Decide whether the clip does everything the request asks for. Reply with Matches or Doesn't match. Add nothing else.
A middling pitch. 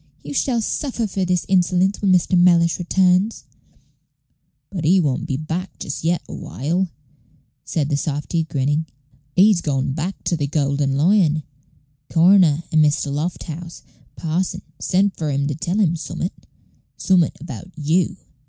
Matches